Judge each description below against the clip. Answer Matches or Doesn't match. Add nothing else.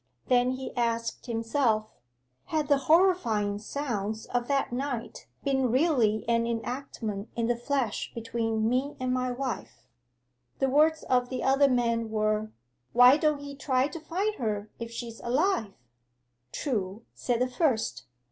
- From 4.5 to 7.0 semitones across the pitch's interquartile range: Doesn't match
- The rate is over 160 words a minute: Doesn't match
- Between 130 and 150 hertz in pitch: Doesn't match